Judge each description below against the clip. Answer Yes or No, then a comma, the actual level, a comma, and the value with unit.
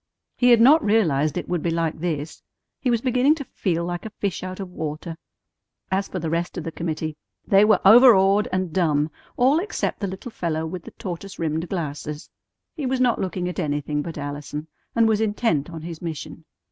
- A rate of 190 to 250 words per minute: Yes, average, 200 wpm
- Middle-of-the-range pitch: Yes, medium, 180 Hz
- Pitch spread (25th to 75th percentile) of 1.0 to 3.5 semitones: No, average, 5.3 semitones